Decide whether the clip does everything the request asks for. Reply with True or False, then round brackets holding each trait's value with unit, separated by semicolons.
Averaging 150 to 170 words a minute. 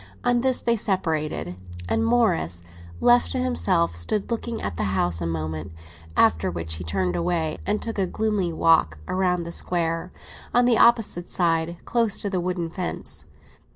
True (165 wpm)